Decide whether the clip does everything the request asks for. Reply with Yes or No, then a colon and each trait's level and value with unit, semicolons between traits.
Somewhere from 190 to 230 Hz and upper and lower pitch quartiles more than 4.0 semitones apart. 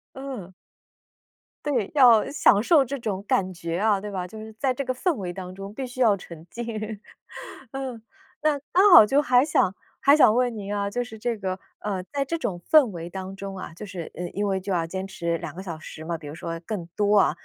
Yes: high, 205 Hz; average, 5.3 semitones